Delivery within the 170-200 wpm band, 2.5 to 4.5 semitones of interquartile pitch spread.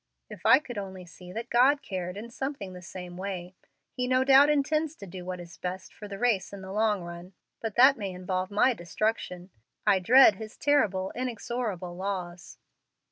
No: average, 190 wpm; average, 5.0 semitones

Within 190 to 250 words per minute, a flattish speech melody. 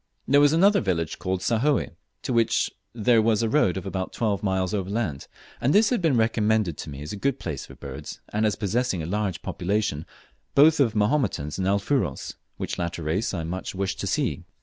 No: average, 200 wpm; average, 4.5 semitones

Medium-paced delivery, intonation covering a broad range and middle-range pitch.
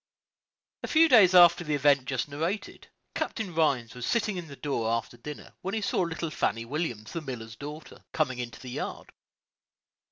Yes: average, 180 wpm; wide, 5.9 semitones; medium, 150 Hz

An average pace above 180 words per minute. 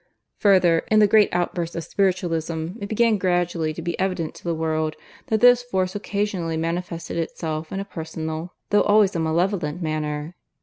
No: average, 170 wpm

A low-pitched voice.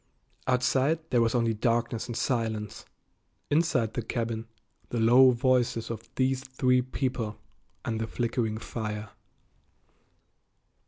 Yes: low, 120 Hz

